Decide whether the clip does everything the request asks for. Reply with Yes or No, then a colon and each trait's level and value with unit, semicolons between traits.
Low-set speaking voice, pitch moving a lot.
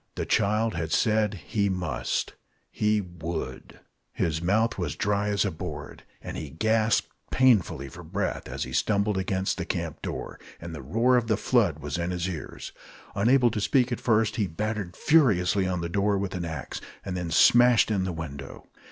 No: low, 100 Hz; average, 4.4 semitones